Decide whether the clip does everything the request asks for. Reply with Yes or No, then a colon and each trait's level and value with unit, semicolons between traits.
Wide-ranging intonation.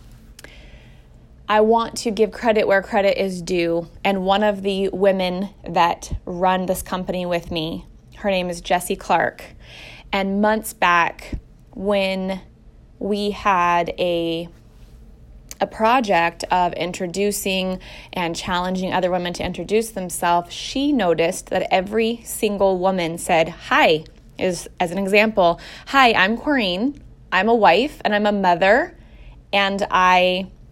No: average, 2.8 semitones